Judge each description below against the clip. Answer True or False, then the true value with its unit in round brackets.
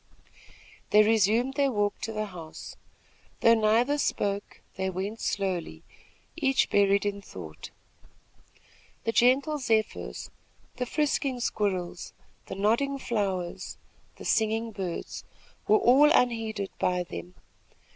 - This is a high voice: True (215 Hz)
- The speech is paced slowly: True (115 wpm)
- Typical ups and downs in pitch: True (3.9 semitones)